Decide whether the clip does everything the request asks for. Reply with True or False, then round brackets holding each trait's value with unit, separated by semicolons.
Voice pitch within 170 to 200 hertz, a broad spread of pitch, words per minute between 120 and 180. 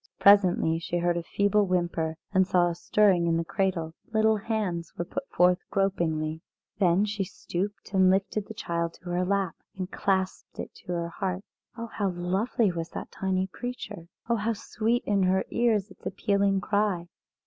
False (190 Hz; 2.9 semitones; 175 wpm)